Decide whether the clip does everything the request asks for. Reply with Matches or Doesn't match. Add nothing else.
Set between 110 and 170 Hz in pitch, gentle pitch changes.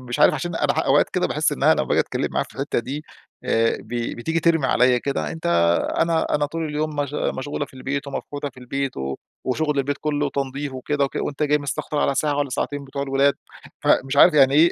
Matches